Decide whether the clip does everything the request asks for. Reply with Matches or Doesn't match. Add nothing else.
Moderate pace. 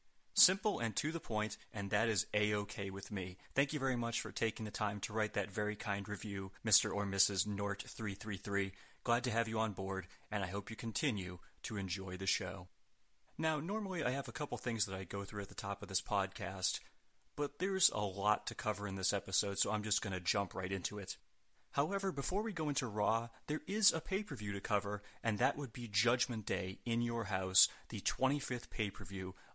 Doesn't match